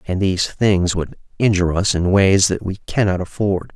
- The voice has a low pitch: Yes, very low, 95 Hz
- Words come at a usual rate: Yes, average, 190 wpm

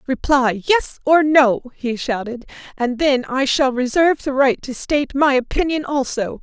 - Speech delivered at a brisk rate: No, average, 170 wpm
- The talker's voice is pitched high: Yes, very high, 265 Hz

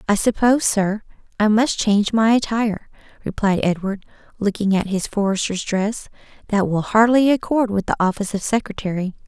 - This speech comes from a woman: Yes, female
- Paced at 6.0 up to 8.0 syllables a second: No, 5.5 syllables/s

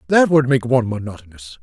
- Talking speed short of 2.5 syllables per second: No, 6.4 syllables/s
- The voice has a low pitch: Yes, low, 120 Hz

